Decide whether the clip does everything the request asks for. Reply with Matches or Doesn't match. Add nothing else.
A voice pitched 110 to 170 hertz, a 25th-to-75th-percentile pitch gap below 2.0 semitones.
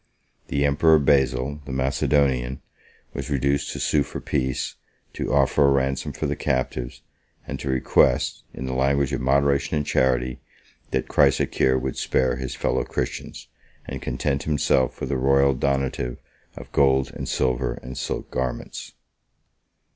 Doesn't match